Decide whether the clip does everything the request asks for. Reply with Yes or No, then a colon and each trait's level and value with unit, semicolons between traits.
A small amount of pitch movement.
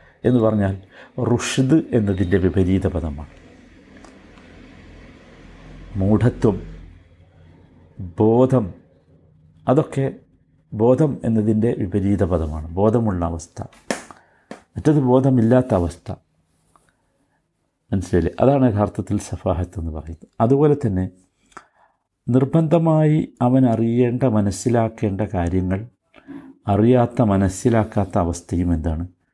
No: average, 5.3 semitones